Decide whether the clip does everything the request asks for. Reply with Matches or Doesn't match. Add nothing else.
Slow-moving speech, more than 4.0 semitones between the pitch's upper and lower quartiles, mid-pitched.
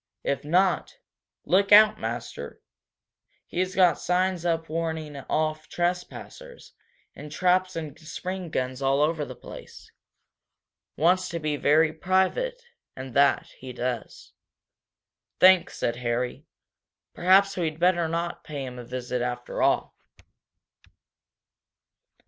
Matches